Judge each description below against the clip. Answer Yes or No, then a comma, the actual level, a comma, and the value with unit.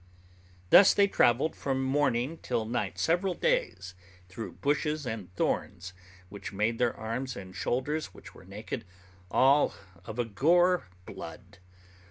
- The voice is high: No, low, 125 Hz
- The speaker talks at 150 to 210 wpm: No, slow, 135 wpm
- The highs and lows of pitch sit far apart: Yes, wide, 5.8 semitones